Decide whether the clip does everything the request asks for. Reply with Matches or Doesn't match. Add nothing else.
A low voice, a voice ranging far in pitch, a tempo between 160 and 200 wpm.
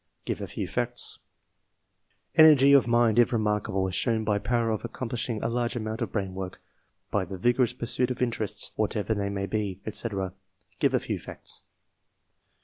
Doesn't match